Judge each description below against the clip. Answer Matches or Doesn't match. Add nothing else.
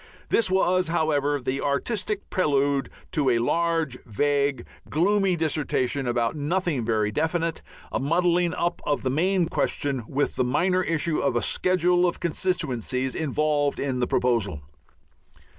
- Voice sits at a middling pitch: Matches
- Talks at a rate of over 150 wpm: Doesn't match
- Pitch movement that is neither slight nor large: Matches